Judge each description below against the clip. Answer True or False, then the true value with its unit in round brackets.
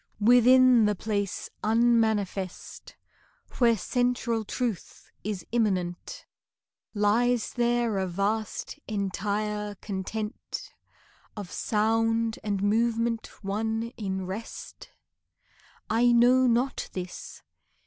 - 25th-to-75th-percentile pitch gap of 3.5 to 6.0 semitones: False (2.6 semitones)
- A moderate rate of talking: False (85 wpm)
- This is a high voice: True (220 Hz)